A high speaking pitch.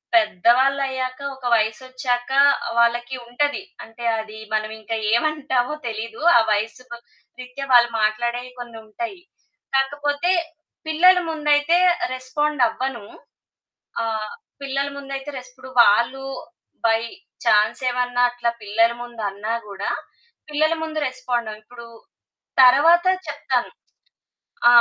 Yes: high, 245 Hz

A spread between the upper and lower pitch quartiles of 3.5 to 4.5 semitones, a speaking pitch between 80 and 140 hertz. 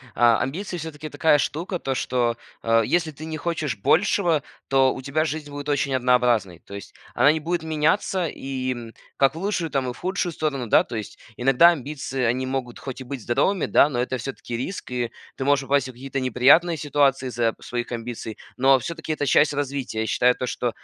Yes: average, 4.1 semitones; low, 135 Hz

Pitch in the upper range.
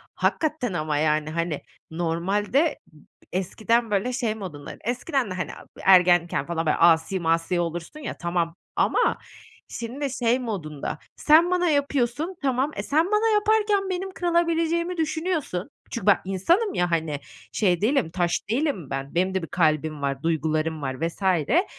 Yes: high, 195 Hz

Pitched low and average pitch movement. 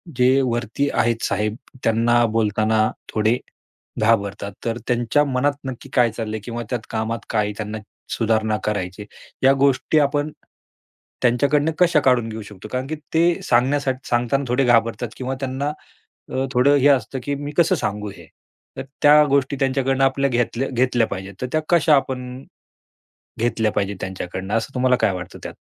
Yes: low, 125 Hz; average, 3.7 semitones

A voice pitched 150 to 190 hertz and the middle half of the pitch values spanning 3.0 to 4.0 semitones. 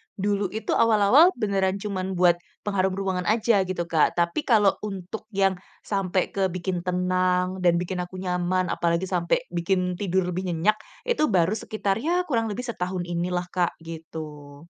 No: medium, 185 Hz; narrow, 2.4 semitones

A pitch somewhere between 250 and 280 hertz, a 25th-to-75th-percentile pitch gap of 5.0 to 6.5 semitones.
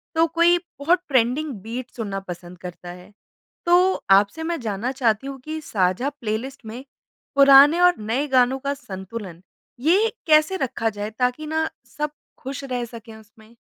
Yes: very high, 255 Hz; wide, 5.6 semitones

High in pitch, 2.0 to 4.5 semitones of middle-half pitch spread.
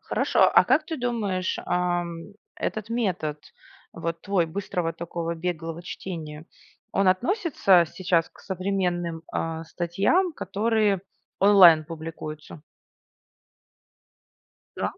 No: medium, 180 Hz; average, 3.4 semitones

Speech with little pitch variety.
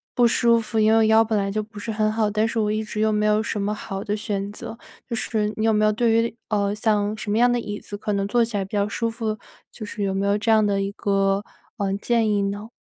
Yes: narrow, 1.5 semitones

